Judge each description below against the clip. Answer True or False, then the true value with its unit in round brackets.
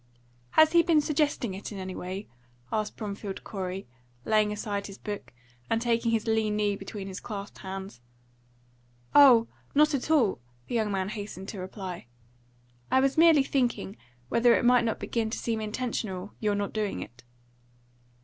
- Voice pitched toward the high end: True (215 Hz)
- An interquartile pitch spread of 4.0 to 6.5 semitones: False (3.4 semitones)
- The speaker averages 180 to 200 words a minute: False (165 wpm)